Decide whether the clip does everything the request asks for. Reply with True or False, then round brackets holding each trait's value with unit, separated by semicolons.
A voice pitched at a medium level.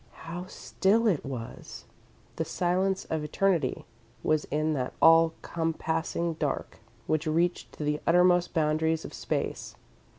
True (165 Hz)